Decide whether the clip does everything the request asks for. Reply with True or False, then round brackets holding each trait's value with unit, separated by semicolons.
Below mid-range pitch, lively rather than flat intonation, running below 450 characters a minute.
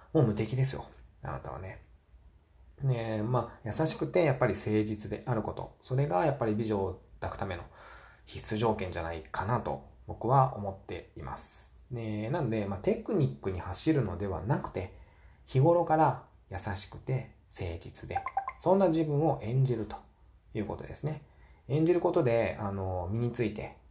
True (110 Hz; 6.4 semitones; 320 characters per minute)